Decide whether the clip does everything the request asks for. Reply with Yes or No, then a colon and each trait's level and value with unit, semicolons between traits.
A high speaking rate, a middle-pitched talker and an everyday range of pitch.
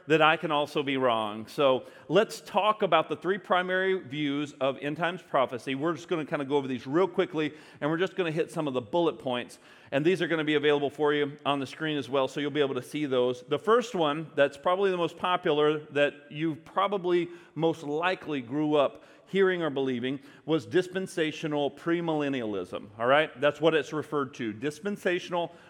Yes: fast, 210 wpm; medium, 150 Hz; average, 3.5 semitones